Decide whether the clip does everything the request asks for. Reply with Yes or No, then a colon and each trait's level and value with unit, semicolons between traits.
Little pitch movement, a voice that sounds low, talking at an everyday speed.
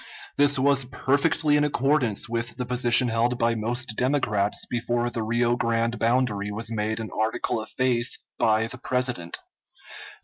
Yes: narrow, 2.3 semitones; low, 120 Hz; average, 150 wpm